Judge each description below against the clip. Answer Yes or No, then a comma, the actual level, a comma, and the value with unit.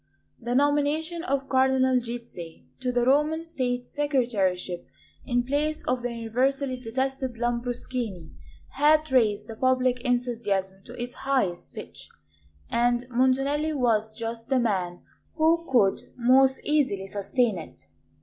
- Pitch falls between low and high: No, very high, 250 Hz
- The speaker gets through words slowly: Yes, slow, 125 wpm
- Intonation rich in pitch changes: No, average, 2.9 semitones